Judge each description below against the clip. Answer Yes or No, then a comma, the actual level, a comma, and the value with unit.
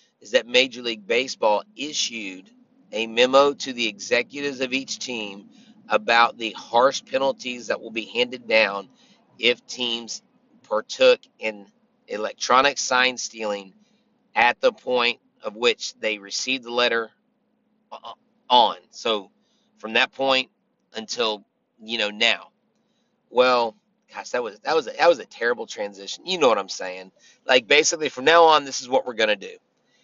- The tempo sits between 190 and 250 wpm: No, average, 150 wpm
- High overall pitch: No, low, 125 Hz